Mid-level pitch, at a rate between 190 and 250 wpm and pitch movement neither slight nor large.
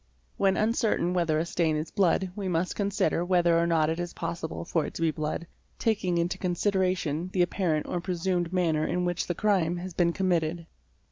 No: medium, 175 Hz; average, 195 wpm; narrow, 2.0 semitones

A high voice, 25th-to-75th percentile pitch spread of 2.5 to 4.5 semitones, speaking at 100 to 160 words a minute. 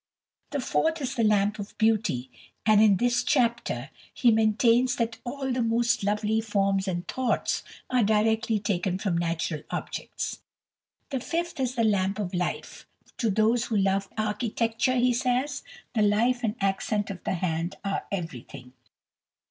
Yes: high, 215 Hz; average, 3.6 semitones; average, 155 wpm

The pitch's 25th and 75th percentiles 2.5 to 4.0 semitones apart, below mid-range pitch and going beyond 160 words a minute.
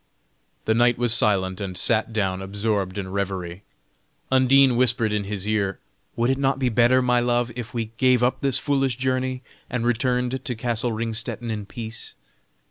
Yes: average, 3.2 semitones; low, 120 Hz; average, 170 wpm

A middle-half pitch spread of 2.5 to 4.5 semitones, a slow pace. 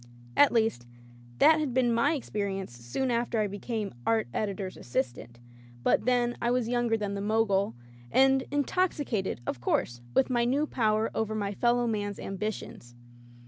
No: average, 3.8 semitones; average, 165 wpm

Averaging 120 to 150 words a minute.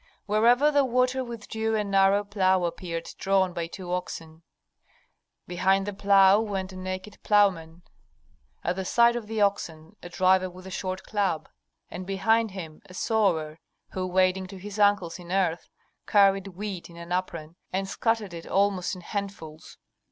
No: average, 160 wpm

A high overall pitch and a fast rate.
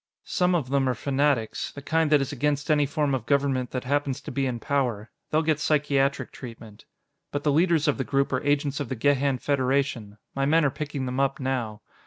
No: medium, 140 Hz; fast, 215 wpm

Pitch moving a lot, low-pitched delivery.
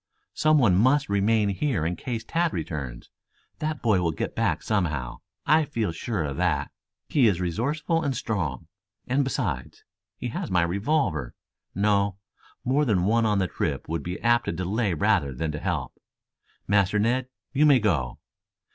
Yes: wide, 7.1 semitones; low, 100 Hz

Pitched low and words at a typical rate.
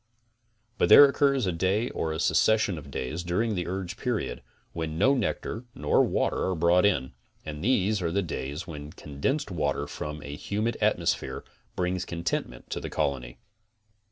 Yes: very low, 90 Hz; average, 165 wpm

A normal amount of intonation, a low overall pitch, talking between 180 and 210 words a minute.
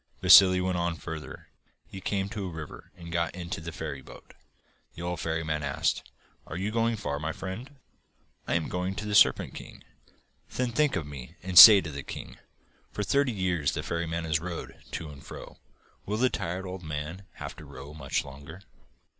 Yes: average, 3.7 semitones; very low, 85 Hz; average, 190 wpm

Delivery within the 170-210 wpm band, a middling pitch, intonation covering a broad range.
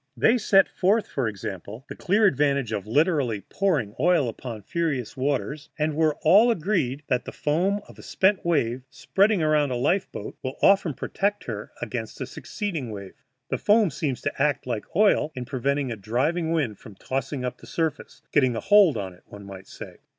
Yes: average, 190 wpm; medium, 145 Hz; wide, 6.6 semitones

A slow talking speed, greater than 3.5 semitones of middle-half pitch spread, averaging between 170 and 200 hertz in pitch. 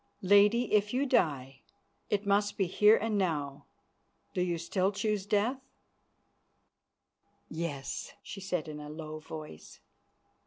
Yes: slow, 125 wpm; average, 5.1 semitones; high, 190 Hz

